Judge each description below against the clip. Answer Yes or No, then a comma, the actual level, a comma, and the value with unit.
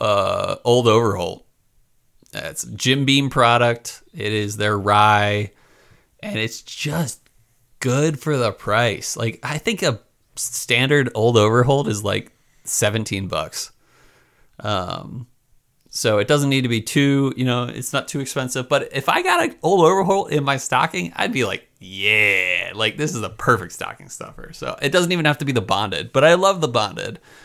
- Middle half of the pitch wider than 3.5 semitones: Yes, average, 4.4 semitones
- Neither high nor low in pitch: No, low, 125 Hz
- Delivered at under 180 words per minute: Yes, average, 170 wpm